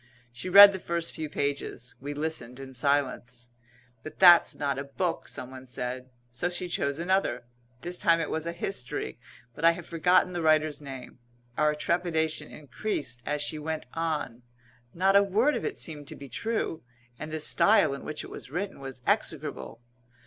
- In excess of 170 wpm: Yes, average, 180 wpm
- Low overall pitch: No, medium, 155 Hz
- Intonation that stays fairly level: No, average, 4.1 semitones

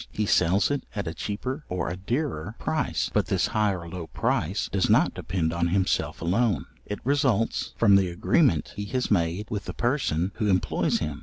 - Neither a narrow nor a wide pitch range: Yes, average, 4.5 semitones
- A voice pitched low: Yes, low, 100 Hz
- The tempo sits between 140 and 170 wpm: No, average, 190 wpm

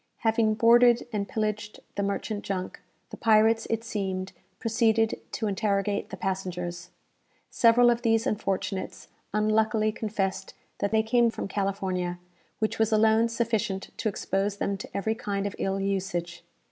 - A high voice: Yes, high, 210 Hz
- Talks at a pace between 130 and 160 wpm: Yes, average, 145 wpm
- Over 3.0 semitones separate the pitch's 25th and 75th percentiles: No, narrow, 2.4 semitones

